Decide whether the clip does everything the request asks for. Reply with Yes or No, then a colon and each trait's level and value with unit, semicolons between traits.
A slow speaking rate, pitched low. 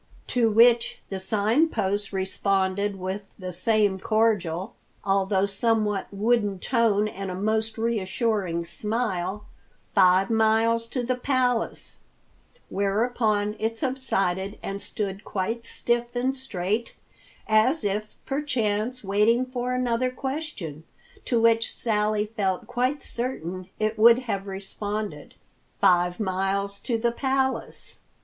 No: slow, 115 wpm; high, 215 Hz